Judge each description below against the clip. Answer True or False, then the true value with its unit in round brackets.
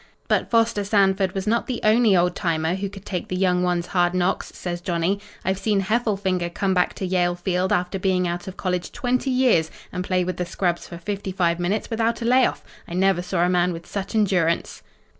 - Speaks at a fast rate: True (215 wpm)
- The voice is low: False (185 Hz)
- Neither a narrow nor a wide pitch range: False (2.3 semitones)